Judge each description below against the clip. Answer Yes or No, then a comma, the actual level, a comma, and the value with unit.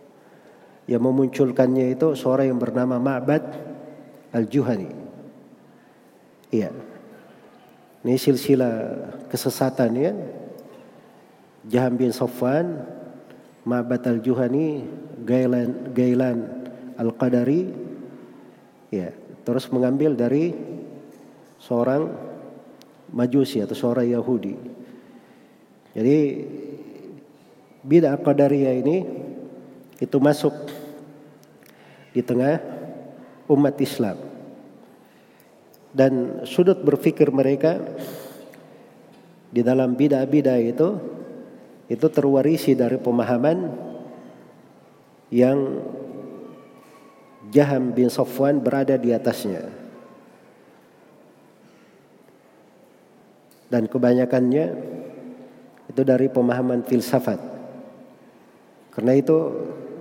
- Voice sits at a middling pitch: No, low, 130 Hz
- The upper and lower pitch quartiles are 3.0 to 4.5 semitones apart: No, narrow, 2.6 semitones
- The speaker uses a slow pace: Yes, slow, 65 wpm